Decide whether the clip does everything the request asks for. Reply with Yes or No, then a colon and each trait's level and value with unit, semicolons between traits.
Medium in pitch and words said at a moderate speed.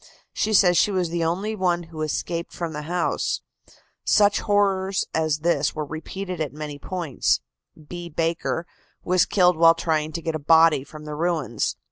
Yes: medium, 170 Hz; average, 170 wpm